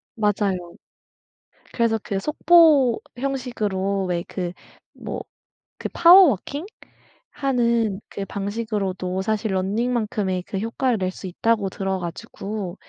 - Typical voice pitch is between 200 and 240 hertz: Yes, high, 210 Hz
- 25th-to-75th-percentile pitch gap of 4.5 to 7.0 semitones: No, average, 4.1 semitones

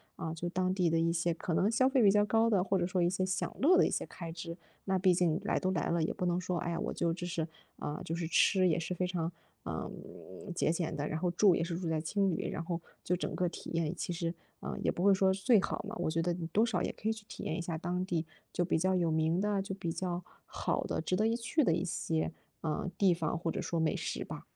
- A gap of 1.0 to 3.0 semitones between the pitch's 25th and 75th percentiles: Yes, narrow, 2.4 semitones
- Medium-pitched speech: Yes, medium, 175 Hz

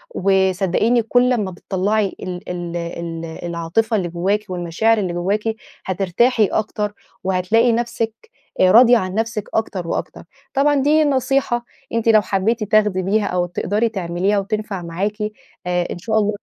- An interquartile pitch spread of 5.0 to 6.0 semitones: No, average, 3.8 semitones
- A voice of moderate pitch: No, high, 205 Hz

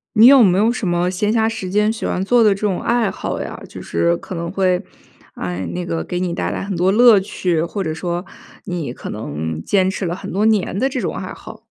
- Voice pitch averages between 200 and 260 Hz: No, medium, 185 Hz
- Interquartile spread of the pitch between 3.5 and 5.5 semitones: Yes, average, 3.9 semitones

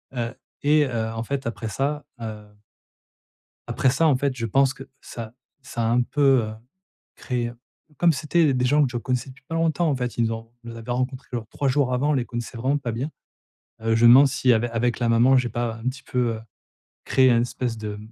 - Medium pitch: No, low, 125 Hz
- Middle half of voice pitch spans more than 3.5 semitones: No, average, 2.9 semitones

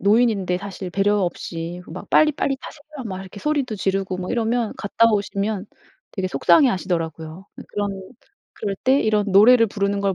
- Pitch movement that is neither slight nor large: Yes, average, 3.6 semitones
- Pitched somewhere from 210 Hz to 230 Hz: No, high, 200 Hz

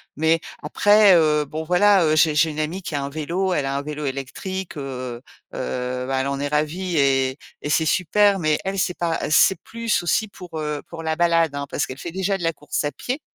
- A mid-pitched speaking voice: Yes, medium, 155 Hz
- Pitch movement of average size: Yes, average, 4.0 semitones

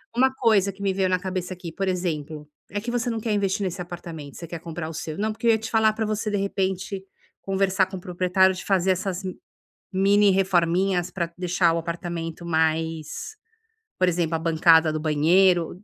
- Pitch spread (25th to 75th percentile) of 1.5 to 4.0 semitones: Yes, average, 2.7 semitones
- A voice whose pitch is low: No, medium, 185 Hz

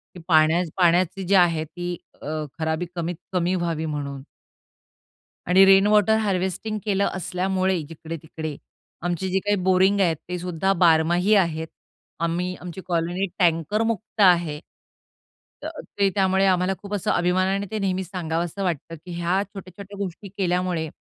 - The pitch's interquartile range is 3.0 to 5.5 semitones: No, narrow, 2.6 semitones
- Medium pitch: Yes, medium, 180 Hz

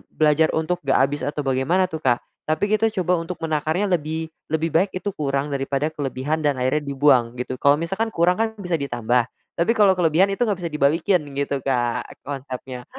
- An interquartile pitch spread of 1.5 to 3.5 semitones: No, average, 4.7 semitones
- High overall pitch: No, medium, 150 Hz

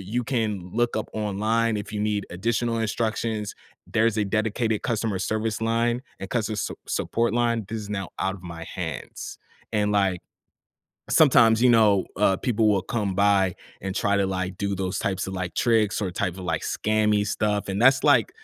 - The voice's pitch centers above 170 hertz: No, low, 105 Hz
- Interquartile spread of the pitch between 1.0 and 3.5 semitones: Yes, average, 2.7 semitones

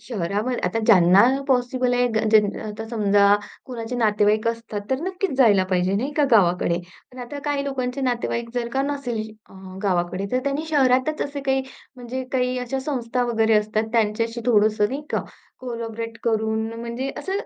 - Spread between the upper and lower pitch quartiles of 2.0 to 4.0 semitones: Yes, average, 3.3 semitones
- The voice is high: Yes, high, 235 Hz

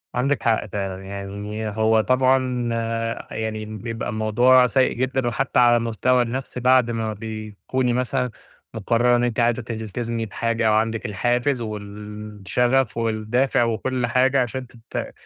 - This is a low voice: Yes, low, 115 Hz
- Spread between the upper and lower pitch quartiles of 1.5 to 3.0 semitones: Yes, narrow, 2.4 semitones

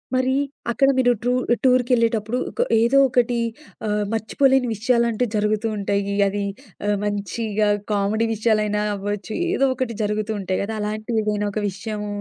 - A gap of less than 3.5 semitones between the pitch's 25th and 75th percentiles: Yes, narrow, 2.6 semitones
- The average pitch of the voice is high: Yes, high, 215 Hz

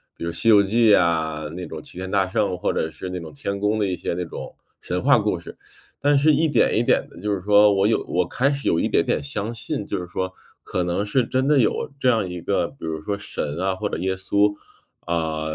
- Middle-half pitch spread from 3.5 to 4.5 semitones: Yes, average, 4.0 semitones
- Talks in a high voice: No, low, 100 Hz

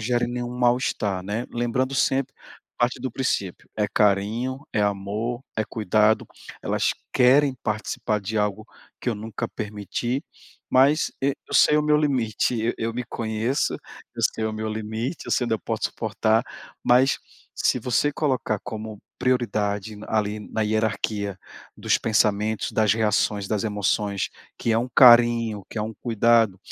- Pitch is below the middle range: Yes, low, 110 Hz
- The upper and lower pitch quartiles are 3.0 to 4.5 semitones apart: No, narrow, 2.6 semitones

